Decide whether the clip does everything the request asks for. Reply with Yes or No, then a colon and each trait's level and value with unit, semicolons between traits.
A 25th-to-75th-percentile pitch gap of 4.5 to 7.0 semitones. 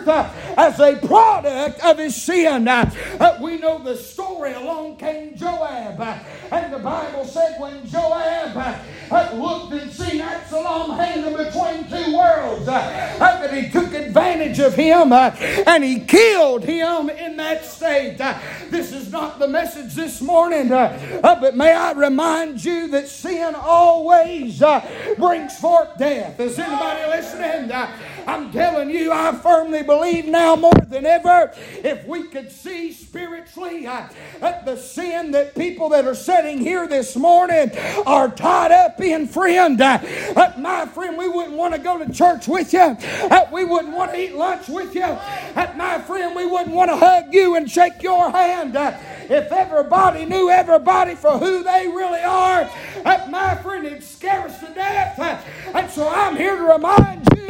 No: average, 2.9 semitones